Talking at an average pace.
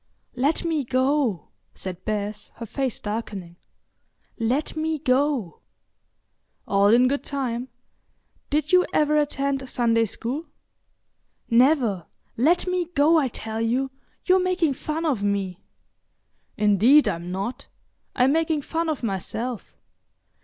No: slow, 120 wpm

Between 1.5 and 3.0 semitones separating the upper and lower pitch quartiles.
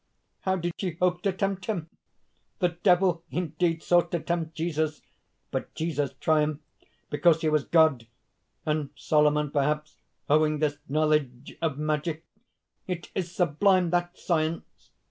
Yes: narrow, 2.4 semitones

